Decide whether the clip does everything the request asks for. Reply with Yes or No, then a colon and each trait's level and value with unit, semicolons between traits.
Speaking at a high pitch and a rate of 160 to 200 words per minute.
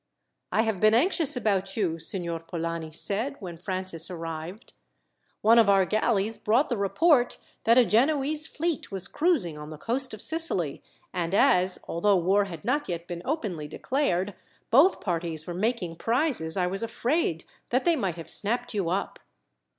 Yes: high, 200 Hz; average, 165 wpm